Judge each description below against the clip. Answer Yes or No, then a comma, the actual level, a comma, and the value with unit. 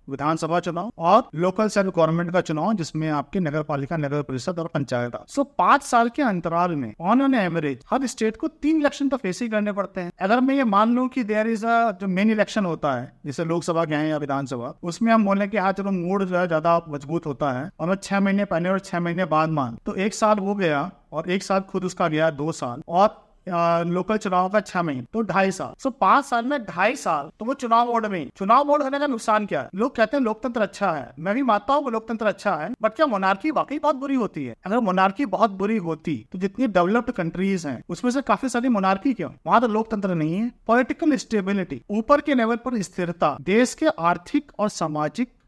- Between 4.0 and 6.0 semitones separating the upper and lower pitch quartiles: Yes, wide, 5.5 semitones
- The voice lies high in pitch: Yes, high, 195 Hz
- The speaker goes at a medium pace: No, fast, 230 wpm